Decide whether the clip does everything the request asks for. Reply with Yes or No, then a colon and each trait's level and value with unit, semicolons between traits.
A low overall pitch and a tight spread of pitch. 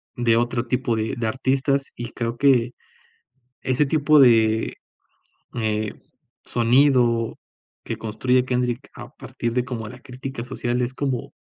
Yes: low, 125 Hz; narrow, 2.1 semitones